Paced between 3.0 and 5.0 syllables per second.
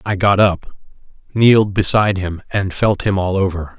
Yes: 4.8 syllables/s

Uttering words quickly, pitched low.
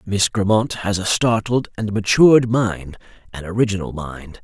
No: average, 150 wpm; low, 105 Hz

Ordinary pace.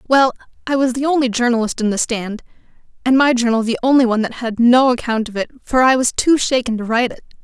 No: fast, 235 wpm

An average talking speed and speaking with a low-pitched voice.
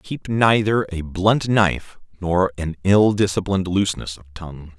Yes: average, 150 wpm; very low, 95 Hz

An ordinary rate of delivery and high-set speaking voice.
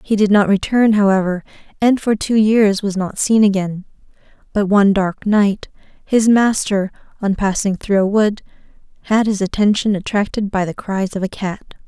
Yes: average, 170 wpm; high, 205 Hz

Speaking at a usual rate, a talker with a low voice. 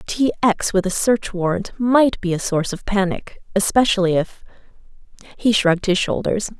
No: average, 155 wpm; high, 200 Hz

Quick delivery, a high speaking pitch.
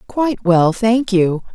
No: average, 155 wpm; high, 205 Hz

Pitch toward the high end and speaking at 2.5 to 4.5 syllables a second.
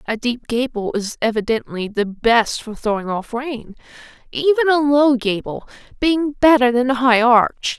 Yes: high, 245 Hz; 4.3 syllables/s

